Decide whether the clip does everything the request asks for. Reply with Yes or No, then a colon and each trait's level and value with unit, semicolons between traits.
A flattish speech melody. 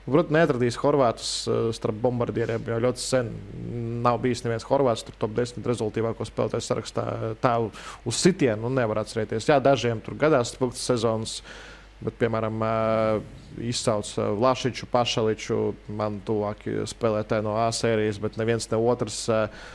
Yes: narrow, 2.1 semitones